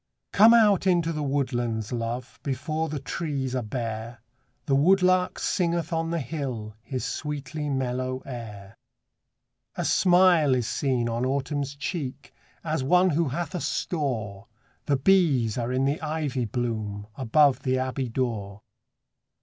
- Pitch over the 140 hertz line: No, low, 135 Hz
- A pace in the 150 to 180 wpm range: No, average, 140 wpm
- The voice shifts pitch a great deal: No, average, 4.8 semitones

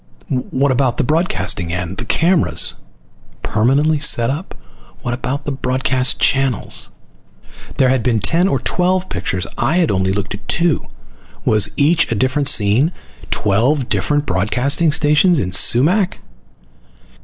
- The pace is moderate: No, slow, 130 wpm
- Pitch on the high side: No, low, 130 Hz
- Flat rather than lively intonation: No, wide, 5.5 semitones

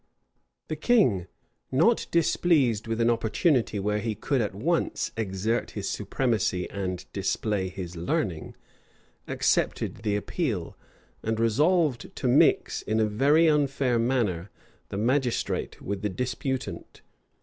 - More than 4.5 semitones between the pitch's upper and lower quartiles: Yes, average, 5.2 semitones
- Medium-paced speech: No, slow, 125 wpm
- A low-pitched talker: Yes, low, 115 Hz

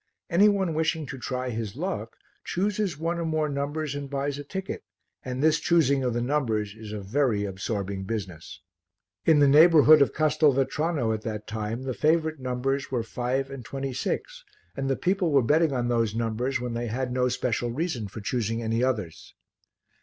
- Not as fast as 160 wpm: No, average, 185 wpm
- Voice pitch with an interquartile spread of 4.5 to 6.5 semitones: Yes, average, 5.1 semitones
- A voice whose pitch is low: Yes, low, 130 Hz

